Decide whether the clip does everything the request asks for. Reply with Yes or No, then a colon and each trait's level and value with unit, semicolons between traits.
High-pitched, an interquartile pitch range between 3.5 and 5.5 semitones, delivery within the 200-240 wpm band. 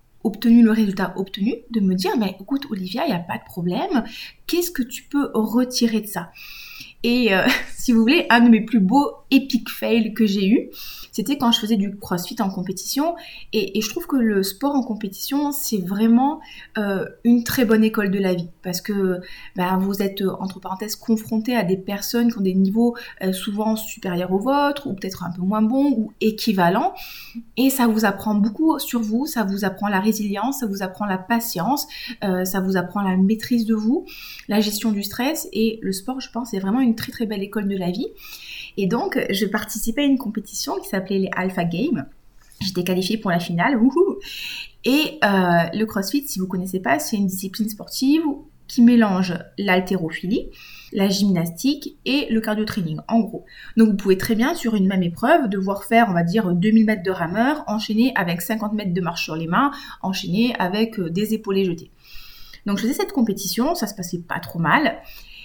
Yes: high, 215 Hz; average, 3.8 semitones; average, 205 wpm